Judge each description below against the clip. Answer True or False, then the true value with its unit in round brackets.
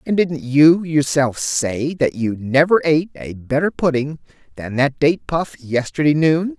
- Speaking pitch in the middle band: True (145 Hz)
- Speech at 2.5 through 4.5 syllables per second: True (4.3 syllables/s)